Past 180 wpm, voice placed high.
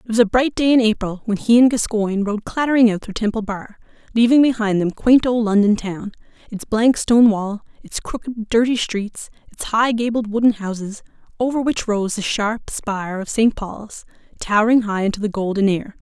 Yes: average, 195 wpm; high, 220 Hz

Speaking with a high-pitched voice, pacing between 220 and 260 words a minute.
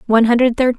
Yes: high, 240 Hz; fast, 230 wpm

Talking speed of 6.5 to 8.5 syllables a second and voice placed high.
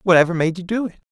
No: 7.5 syllables/s; medium, 180 Hz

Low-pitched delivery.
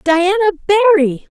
No: very high, 365 Hz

